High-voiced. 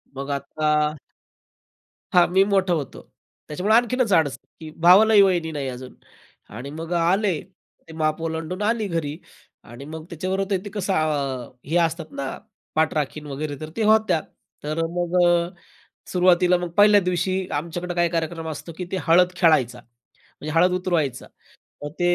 No: medium, 165 Hz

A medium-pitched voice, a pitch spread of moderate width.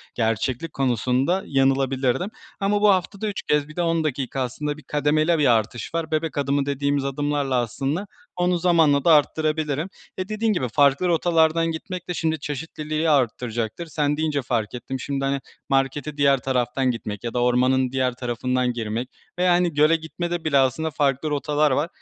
Yes: medium, 145 Hz; average, 3.7 semitones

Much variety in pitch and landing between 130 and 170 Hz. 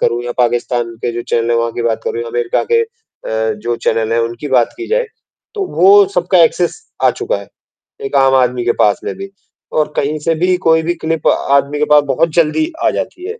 Yes: wide, 7.1 semitones; medium, 140 Hz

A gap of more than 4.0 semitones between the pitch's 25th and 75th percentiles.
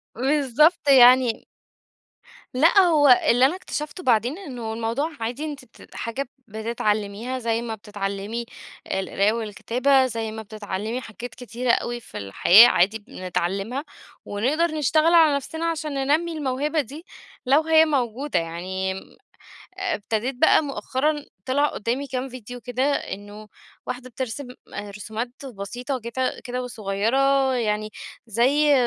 Yes: average, 4.5 semitones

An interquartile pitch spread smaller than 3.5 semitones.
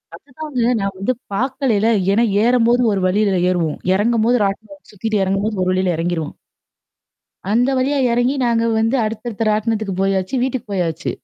No: average, 3.9 semitones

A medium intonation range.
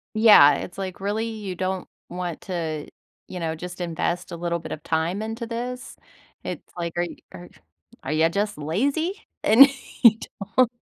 Yes: average, 4.8 semitones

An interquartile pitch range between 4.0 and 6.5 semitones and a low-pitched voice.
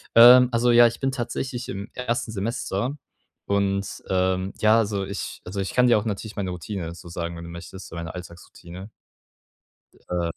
Yes: average, 4.6 semitones; low, 100 Hz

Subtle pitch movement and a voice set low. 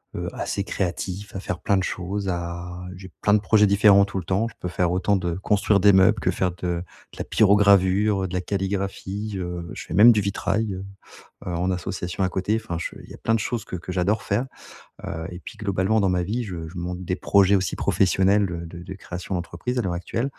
Yes: narrow, 2.3 semitones; very low, 95 Hz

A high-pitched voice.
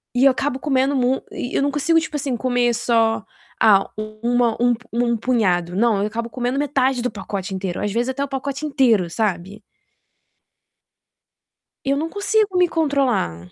Yes: high, 245 Hz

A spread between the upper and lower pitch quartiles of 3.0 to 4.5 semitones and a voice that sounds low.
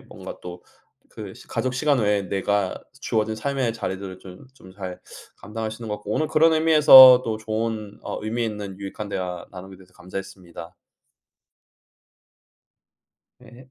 Yes: average, 3.9 semitones; low, 105 Hz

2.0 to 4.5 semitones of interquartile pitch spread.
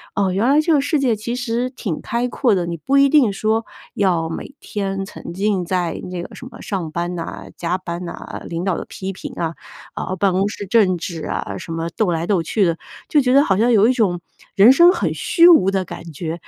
No: wide, 5.5 semitones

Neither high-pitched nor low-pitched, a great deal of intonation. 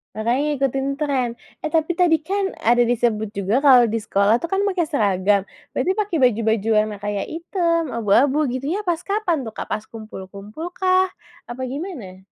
No: very high, 260 Hz; wide, 7.5 semitones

